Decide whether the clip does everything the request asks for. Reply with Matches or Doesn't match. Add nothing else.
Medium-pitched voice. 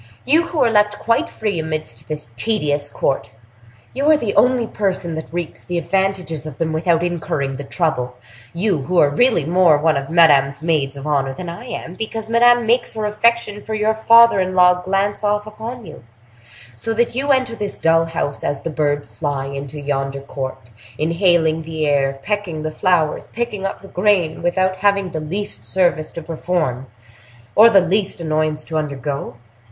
Matches